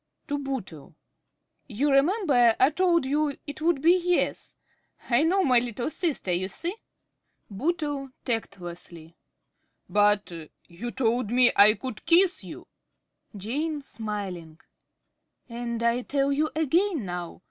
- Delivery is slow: Yes, slow, 125 wpm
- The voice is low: No, very high, 255 Hz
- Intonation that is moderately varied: No, wide, 6.8 semitones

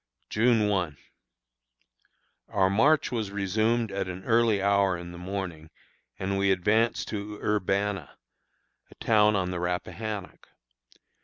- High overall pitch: No, low, 100 Hz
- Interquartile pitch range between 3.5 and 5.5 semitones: No, narrow, 2.6 semitones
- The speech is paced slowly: Yes, slow, 125 wpm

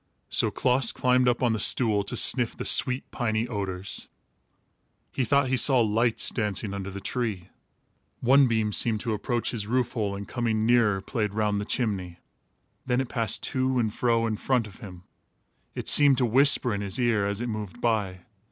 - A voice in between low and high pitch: No, low, 115 Hz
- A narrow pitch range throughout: No, average, 3.1 semitones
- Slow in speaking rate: No, average, 190 wpm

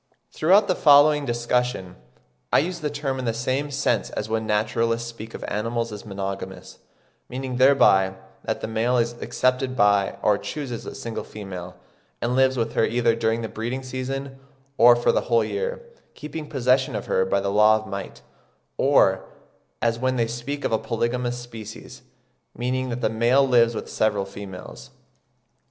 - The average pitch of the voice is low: Yes, low, 120 Hz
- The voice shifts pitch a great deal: No, average, 3.2 semitones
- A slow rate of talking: No, average, 170 wpm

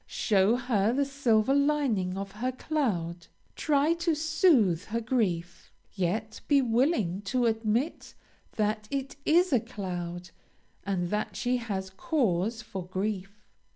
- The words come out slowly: Yes, slow, 130 wpm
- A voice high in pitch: Yes, high, 220 Hz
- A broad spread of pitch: Yes, wide, 6.1 semitones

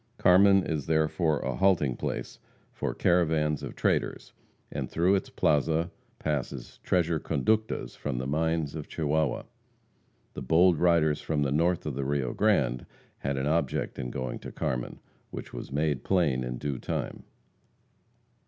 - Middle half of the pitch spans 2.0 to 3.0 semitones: No, average, 3.6 semitones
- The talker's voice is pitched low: Yes, very low, 75 Hz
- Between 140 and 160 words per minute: Yes, average, 150 wpm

